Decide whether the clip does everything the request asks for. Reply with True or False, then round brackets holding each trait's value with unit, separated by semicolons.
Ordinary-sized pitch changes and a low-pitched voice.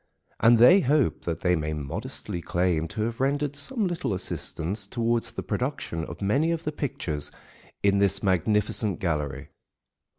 False (7.8 semitones; 105 Hz)